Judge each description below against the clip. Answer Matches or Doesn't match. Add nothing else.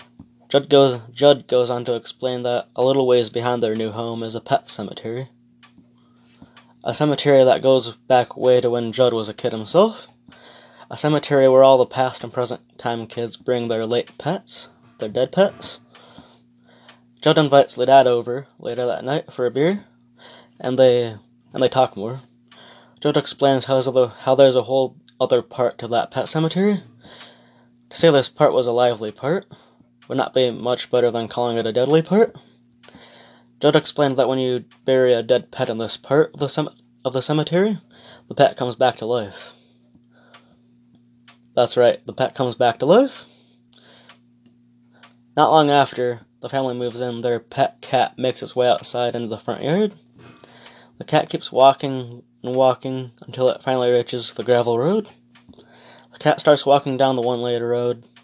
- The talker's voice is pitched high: Doesn't match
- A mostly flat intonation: Matches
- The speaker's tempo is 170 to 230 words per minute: Matches